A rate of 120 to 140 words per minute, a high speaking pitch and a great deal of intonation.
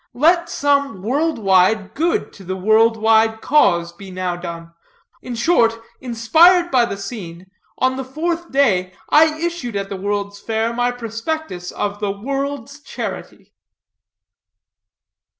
Yes: slow, 135 wpm; high, 225 Hz; wide, 6.1 semitones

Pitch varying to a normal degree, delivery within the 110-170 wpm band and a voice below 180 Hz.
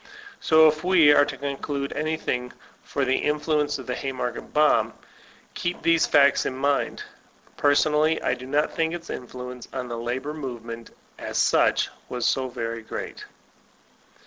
Yes: average, 3.3 semitones; average, 150 wpm; medium, 140 Hz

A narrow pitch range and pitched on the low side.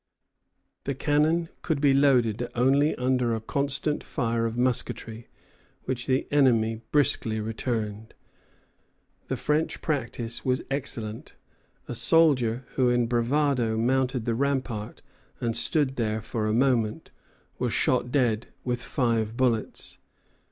No: average, 3.3 semitones; low, 125 Hz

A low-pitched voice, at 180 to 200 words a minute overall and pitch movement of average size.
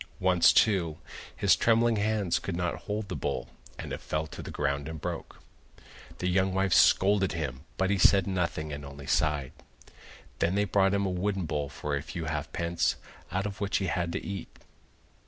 Yes: very low, 90 Hz; average, 190 wpm; average, 4.1 semitones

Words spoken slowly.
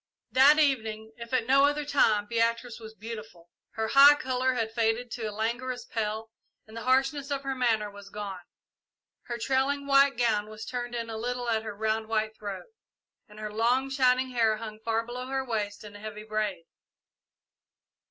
No: average, 180 wpm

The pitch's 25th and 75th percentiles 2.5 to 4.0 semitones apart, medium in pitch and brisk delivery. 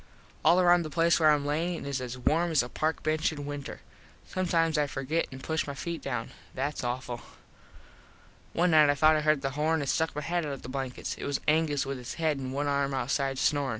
Yes: average, 2.8 semitones; medium, 145 Hz; fast, 230 wpm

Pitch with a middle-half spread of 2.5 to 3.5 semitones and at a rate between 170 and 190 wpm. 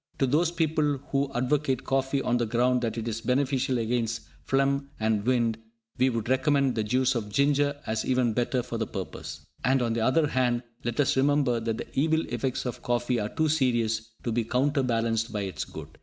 No: average, 3.0 semitones; average, 200 wpm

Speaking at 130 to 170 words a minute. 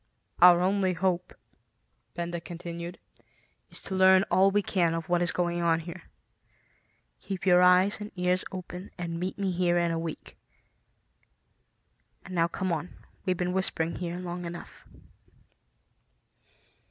Yes: average, 140 wpm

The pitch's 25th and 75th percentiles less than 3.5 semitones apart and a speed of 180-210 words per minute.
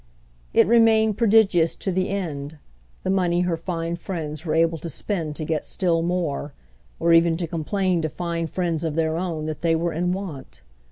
Yes: narrow, 2.5 semitones; average, 185 wpm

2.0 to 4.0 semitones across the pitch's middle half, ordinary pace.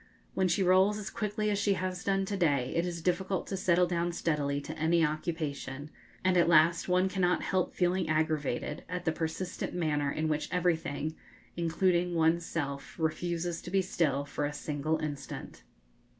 Yes: average, 2.9 semitones; average, 175 wpm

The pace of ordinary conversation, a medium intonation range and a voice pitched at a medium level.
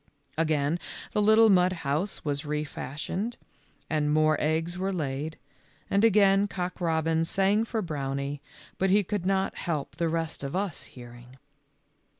Yes: average, 150 wpm; average, 4.6 semitones; medium, 165 Hz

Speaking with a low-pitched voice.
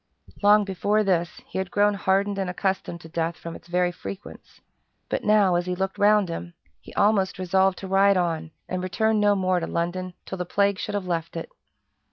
No: high, 190 Hz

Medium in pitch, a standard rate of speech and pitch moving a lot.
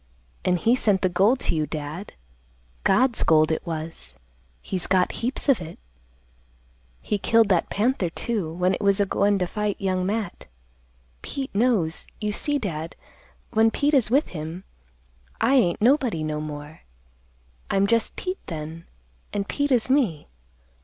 No: high, 200 Hz; average, 155 wpm; wide, 5.8 semitones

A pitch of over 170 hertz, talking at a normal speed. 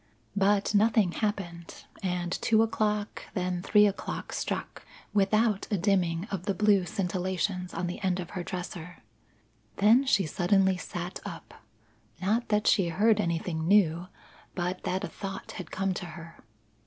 Yes: high, 190 Hz; average, 150 wpm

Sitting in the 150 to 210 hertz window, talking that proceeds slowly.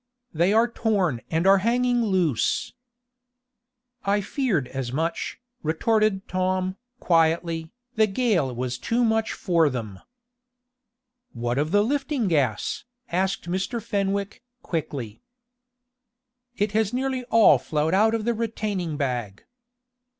Yes: high, 190 Hz; slow, 120 wpm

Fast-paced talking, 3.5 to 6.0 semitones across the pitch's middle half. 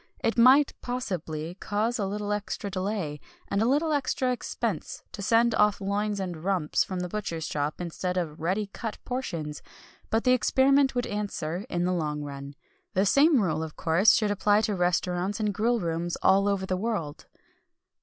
No: average, 175 wpm; average, 4.5 semitones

